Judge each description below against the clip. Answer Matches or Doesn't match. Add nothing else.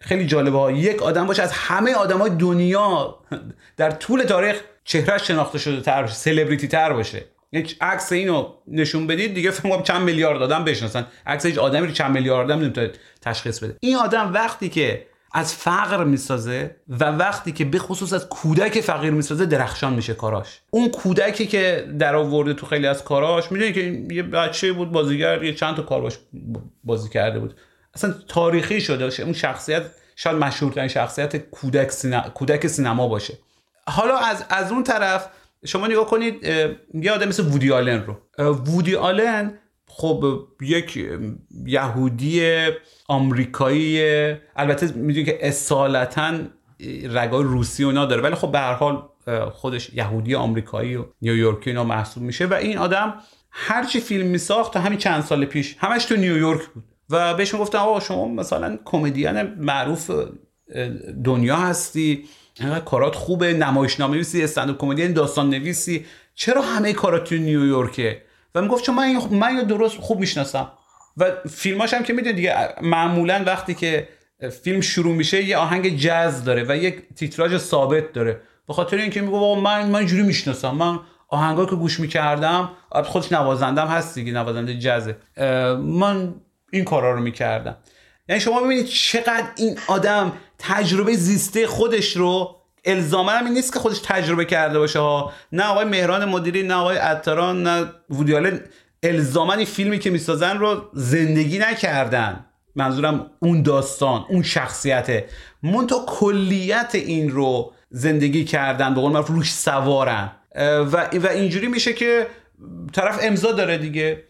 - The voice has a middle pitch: Matches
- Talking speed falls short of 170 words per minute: Matches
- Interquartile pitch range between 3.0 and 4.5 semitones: Doesn't match